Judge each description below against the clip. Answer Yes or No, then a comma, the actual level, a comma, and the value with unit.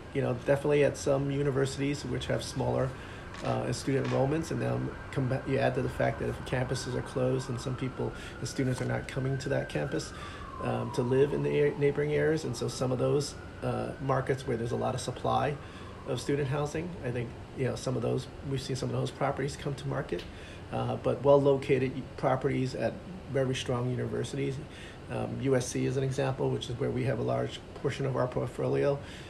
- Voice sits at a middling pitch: No, low, 130 Hz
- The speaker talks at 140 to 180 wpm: No, fast, 205 wpm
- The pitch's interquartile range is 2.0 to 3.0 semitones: Yes, average, 2.7 semitones